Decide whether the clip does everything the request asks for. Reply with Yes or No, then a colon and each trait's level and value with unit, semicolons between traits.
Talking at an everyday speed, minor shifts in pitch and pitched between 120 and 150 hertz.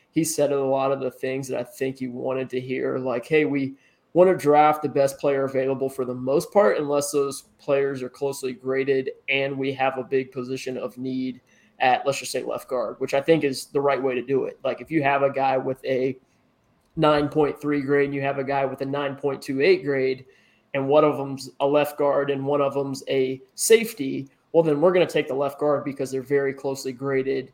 No: fast, 225 wpm; narrow, 1.4 semitones; low, 135 Hz